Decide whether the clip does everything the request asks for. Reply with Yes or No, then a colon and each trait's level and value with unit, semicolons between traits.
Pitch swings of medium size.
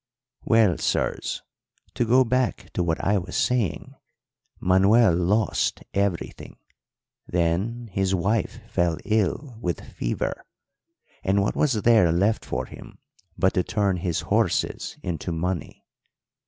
Yes: average, 4.3 semitones